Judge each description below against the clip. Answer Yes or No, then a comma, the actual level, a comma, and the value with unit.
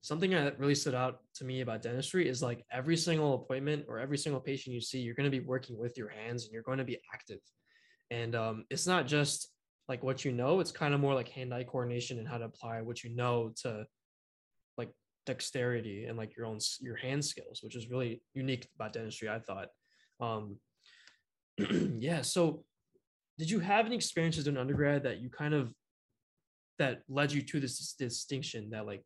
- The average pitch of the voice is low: Yes, low, 130 Hz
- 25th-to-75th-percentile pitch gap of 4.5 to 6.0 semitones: No, average, 3.5 semitones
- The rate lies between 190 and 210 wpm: Yes, average, 200 wpm